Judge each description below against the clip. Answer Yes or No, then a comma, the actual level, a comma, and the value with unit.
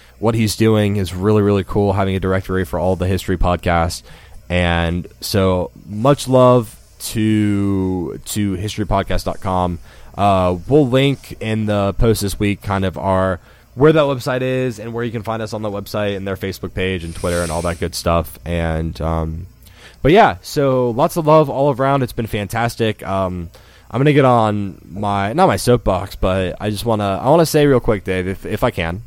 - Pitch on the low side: Yes, low, 100 Hz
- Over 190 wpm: Yes, average, 200 wpm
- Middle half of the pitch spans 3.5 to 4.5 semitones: Yes, average, 4.0 semitones